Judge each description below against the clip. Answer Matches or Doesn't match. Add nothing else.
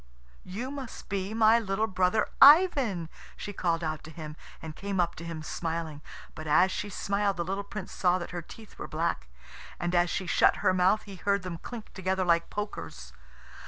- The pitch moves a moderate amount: Matches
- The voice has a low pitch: Doesn't match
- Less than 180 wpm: Doesn't match